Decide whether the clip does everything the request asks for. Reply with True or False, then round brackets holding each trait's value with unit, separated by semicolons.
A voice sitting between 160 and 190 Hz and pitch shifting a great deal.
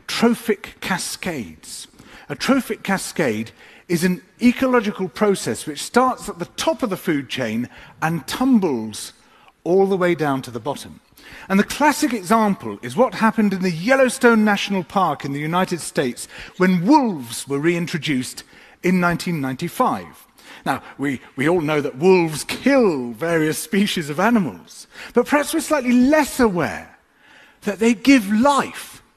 True (185 Hz; 7.4 semitones)